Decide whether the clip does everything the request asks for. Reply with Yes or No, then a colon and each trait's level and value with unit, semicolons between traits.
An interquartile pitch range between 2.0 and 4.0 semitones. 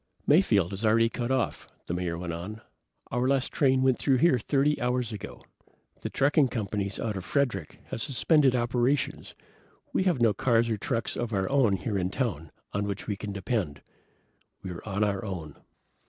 No: average, 4.9 semitones